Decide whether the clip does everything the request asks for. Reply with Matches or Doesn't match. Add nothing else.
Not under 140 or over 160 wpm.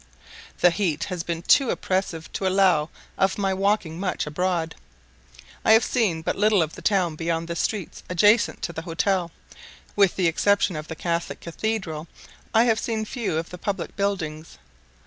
Doesn't match